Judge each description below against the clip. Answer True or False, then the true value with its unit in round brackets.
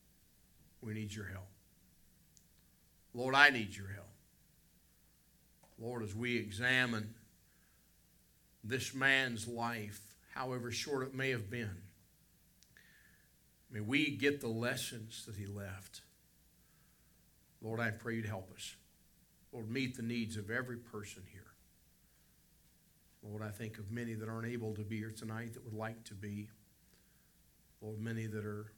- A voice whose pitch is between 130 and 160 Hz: False (110 Hz)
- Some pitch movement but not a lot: False (2.3 semitones)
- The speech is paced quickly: False (135 wpm)